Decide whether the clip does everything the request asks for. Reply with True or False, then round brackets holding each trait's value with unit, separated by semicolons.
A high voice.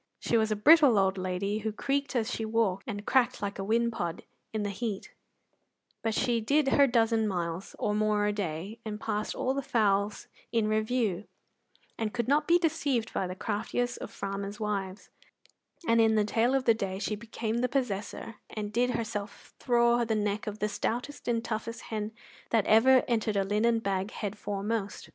True (220 Hz)